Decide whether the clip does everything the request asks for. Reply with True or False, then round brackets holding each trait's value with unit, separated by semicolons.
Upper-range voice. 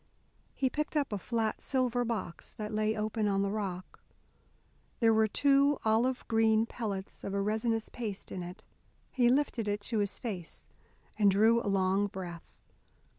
True (220 Hz)